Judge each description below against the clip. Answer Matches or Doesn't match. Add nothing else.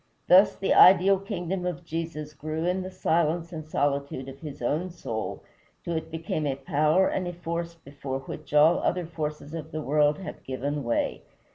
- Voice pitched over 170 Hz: Doesn't match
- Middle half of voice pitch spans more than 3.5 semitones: Doesn't match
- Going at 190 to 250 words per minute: Doesn't match